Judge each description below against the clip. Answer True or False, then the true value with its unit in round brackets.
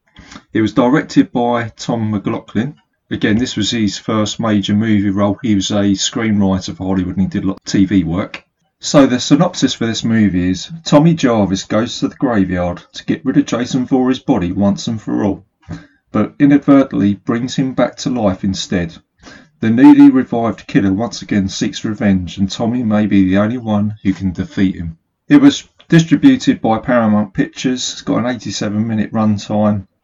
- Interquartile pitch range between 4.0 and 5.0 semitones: True (4.4 semitones)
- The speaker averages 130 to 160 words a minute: False (180 wpm)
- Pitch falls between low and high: False (105 Hz)